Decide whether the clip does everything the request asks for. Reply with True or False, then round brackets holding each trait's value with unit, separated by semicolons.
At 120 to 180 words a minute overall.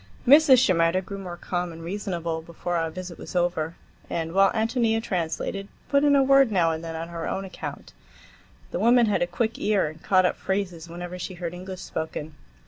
False (200 wpm)